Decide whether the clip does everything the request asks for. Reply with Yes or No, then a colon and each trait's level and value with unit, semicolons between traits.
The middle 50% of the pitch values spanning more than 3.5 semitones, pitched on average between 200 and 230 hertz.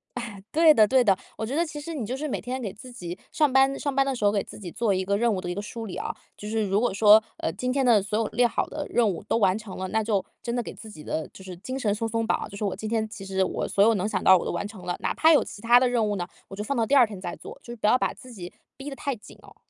Yes: average, 4.0 semitones; high, 220 Hz